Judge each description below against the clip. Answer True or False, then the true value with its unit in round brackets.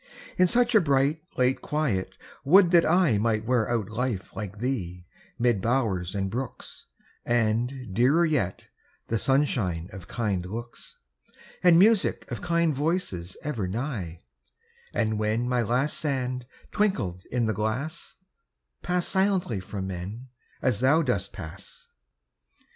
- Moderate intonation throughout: False (6.5 semitones)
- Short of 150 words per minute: True (135 wpm)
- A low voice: True (125 Hz)